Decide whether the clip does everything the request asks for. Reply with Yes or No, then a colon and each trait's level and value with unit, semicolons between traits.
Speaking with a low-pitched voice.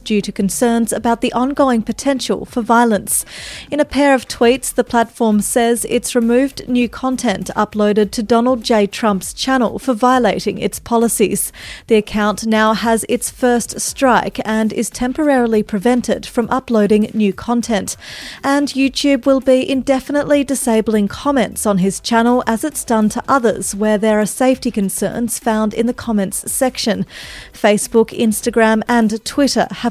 No: high, 235 Hz